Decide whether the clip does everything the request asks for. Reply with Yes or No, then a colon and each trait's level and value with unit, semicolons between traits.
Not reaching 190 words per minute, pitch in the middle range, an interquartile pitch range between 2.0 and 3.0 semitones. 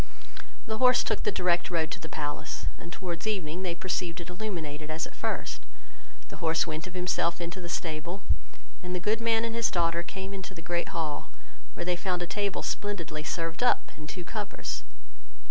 No: average, 195 wpm; medium, 175 Hz; average, 2.7 semitones